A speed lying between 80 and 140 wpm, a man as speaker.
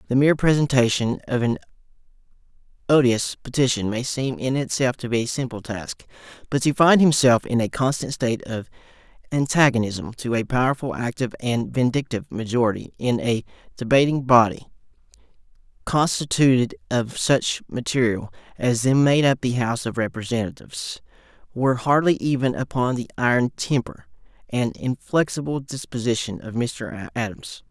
Yes: slow, 135 wpm; male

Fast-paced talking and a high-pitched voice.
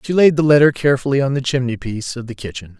No: fast, 260 wpm; low, 130 Hz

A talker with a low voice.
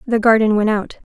No: high, 220 Hz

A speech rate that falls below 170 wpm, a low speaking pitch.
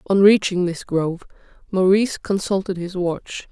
No: slow, 135 wpm; medium, 185 Hz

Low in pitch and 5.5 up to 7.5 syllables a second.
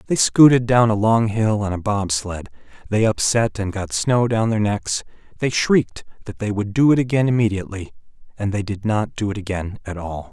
No: low, 105 Hz; 5.2 syllables/s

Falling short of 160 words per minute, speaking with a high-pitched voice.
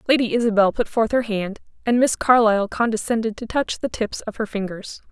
No: average, 200 wpm; high, 225 Hz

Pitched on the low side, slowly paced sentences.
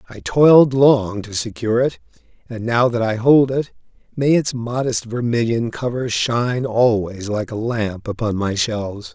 No: low, 115 Hz; average, 165 wpm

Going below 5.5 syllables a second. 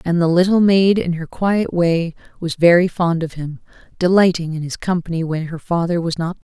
Yes: 5.3 syllables/s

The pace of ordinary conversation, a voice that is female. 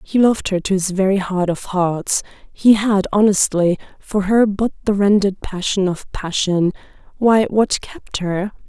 Yes: average, 160 wpm; female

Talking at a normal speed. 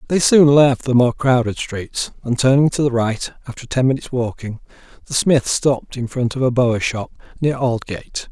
Yes: average, 195 wpm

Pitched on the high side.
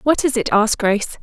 Yes: high, 230 Hz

